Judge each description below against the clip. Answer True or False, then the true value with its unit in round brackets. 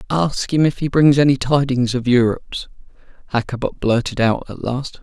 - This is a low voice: True (130 Hz)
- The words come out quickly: False (165 wpm)